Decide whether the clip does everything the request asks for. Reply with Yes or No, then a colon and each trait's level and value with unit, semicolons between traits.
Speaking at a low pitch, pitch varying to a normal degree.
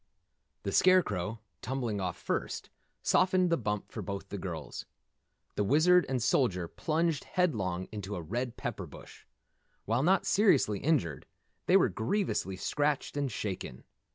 No: low, 120 Hz; wide, 8.4 semitones